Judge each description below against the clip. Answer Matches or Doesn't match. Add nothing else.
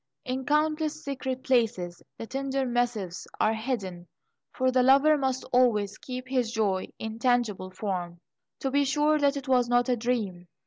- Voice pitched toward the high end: Matches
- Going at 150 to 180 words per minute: Matches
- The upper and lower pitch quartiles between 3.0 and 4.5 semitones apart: Matches